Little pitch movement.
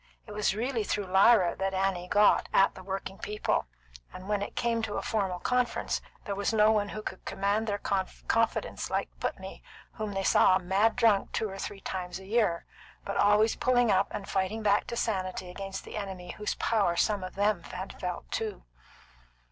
Yes: narrow, 2.1 semitones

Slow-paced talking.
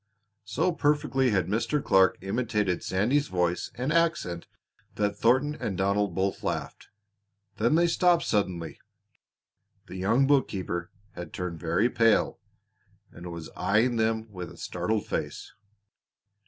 Yes: slow, 130 wpm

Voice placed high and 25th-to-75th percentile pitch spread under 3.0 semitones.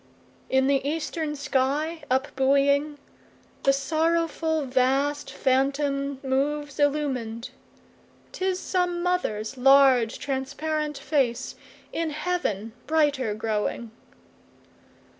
Yes: very high, 280 Hz; narrow, 2.6 semitones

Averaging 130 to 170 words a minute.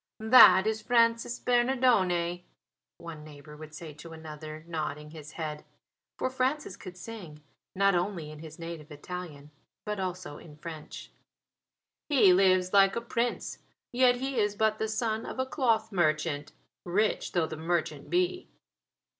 Yes: average, 145 wpm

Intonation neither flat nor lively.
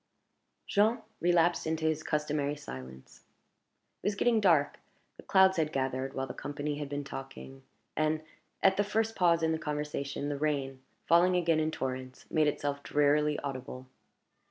Yes: average, 3.2 semitones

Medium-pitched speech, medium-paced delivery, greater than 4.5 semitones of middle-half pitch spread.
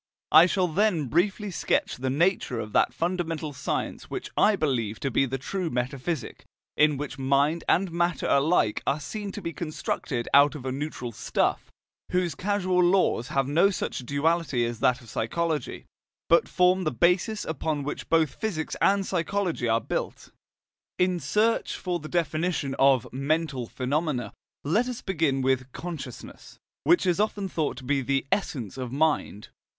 Yes: medium, 155 Hz; average, 165 wpm; average, 5.1 semitones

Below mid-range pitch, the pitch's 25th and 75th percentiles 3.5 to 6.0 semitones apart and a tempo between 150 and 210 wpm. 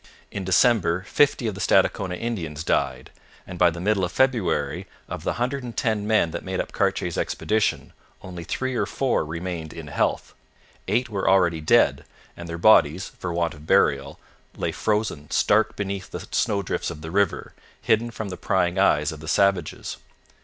Yes: very low, 95 Hz; average, 4.5 semitones; average, 175 wpm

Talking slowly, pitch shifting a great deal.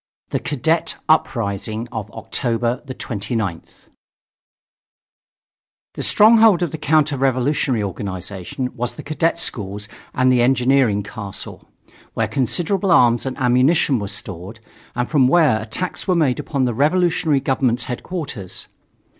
Yes: slow, 120 wpm; wide, 5.7 semitones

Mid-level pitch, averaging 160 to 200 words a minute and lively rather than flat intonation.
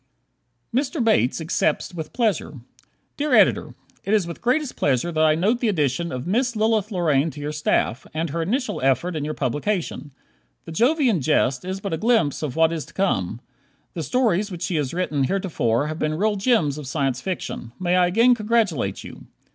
Yes: medium, 175 Hz; average, 185 wpm; wide, 6.3 semitones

